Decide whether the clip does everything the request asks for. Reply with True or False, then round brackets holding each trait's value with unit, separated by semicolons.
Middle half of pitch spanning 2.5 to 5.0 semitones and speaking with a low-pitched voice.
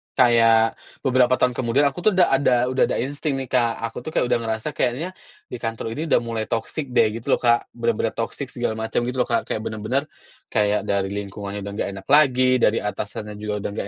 True (2.8 semitones; 115 Hz)